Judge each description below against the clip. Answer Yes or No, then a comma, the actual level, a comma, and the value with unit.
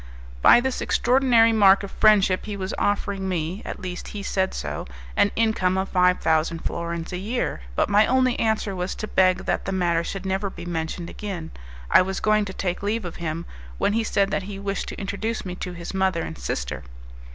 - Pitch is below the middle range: No, high, 190 Hz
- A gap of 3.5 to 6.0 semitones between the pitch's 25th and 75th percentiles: No, average, 2.9 semitones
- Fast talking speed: Yes, fast, 210 wpm